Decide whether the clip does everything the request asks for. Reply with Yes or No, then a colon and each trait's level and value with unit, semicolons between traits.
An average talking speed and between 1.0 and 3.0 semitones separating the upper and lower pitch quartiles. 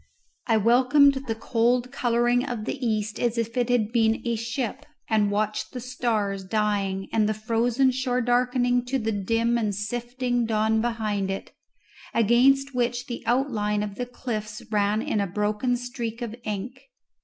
Yes: average, 165 wpm; narrow, 2.5 semitones